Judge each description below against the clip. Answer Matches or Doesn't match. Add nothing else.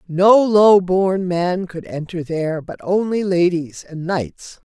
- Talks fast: Doesn't match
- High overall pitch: Doesn't match